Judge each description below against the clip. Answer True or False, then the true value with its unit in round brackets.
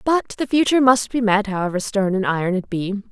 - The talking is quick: True (230 wpm)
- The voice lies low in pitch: False (215 Hz)